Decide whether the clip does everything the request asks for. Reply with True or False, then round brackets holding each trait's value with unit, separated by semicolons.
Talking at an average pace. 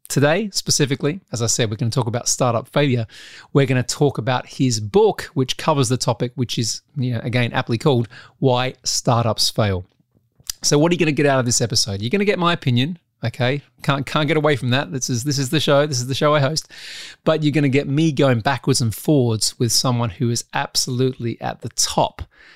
False (230 wpm)